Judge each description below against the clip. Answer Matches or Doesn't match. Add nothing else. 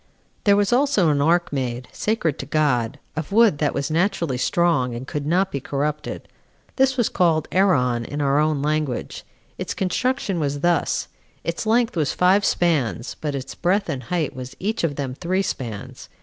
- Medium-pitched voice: Matches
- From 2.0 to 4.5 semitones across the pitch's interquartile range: Doesn't match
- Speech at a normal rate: Matches